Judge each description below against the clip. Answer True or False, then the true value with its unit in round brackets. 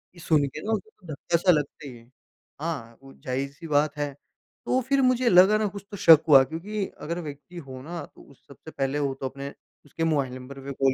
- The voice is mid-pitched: True (150 Hz)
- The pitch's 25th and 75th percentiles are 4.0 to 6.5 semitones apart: True (4.4 semitones)